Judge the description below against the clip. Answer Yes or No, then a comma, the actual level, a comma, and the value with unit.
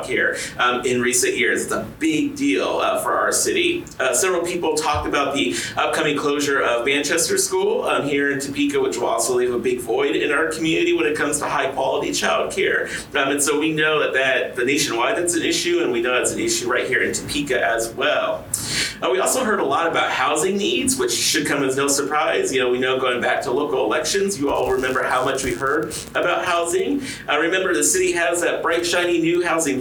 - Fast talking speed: Yes, fast, 225 wpm